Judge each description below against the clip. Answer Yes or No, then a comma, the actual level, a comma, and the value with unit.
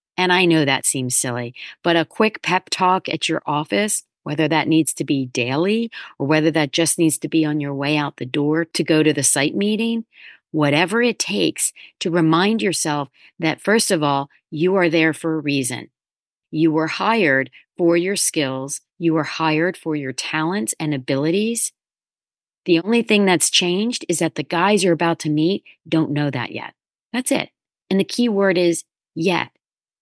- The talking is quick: No, average, 190 wpm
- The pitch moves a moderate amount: Yes, average, 3.8 semitones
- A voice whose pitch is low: No, medium, 160 Hz